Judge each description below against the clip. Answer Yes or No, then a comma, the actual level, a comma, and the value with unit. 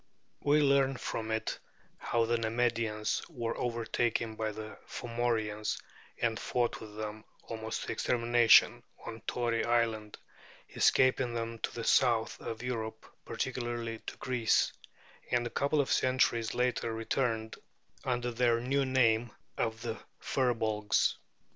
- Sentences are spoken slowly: Yes, slow, 130 wpm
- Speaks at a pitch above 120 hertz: No, low, 115 Hz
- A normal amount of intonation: No, narrow, 1.7 semitones